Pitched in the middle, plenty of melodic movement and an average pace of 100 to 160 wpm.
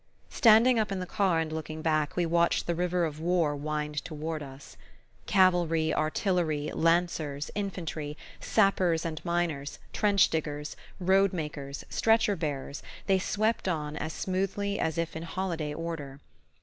No: medium, 165 Hz; average, 3.5 semitones; average, 145 wpm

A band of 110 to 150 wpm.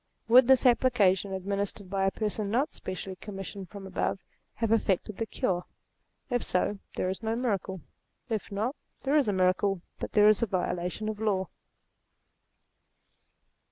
No: average, 160 wpm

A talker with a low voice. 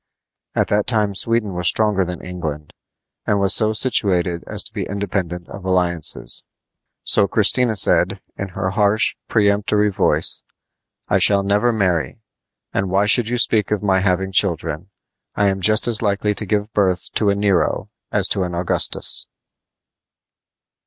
Yes: low, 100 Hz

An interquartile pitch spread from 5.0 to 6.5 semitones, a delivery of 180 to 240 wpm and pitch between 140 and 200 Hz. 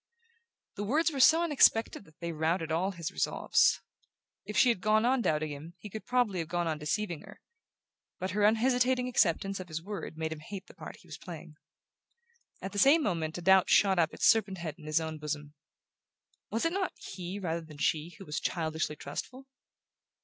Yes: wide, 5.5 semitones; average, 200 wpm; medium, 185 Hz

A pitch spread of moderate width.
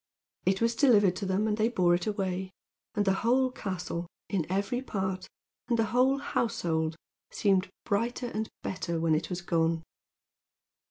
Yes: average, 4.2 semitones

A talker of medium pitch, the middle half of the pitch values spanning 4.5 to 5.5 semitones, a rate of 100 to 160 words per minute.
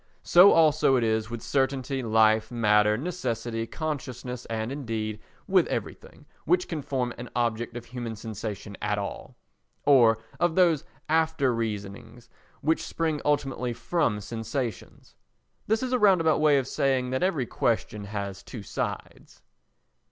No: low, 125 Hz; average, 5.0 semitones; average, 145 wpm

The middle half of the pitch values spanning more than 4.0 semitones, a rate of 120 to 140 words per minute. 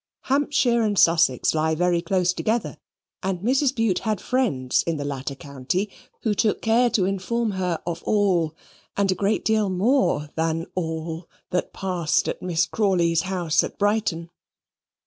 No: average, 4.7 semitones; average, 155 wpm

